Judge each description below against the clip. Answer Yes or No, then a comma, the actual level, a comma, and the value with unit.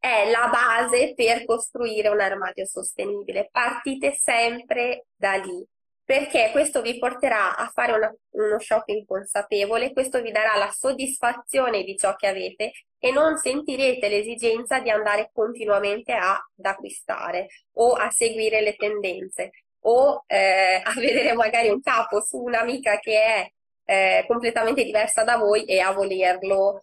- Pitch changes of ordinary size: Yes, average, 3.7 semitones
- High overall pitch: Yes, high, 225 Hz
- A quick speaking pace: No, average, 145 wpm